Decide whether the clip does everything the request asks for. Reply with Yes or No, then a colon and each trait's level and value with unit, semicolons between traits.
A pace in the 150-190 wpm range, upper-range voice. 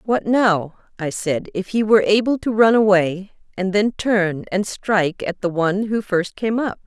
No: average, 200 wpm; high, 200 Hz